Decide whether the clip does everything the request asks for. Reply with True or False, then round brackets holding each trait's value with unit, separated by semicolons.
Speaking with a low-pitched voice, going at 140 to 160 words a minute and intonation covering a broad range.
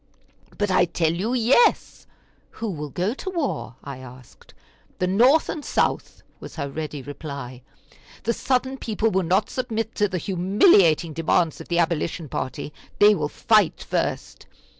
False (180 Hz; 155 wpm; 6.4 semitones)